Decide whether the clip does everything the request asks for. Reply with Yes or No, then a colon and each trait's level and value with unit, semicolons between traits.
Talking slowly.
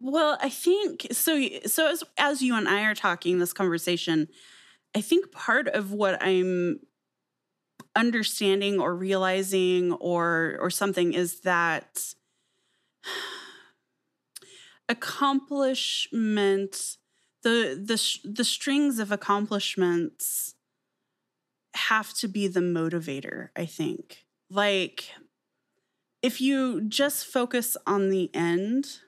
Yes: slow, 105 wpm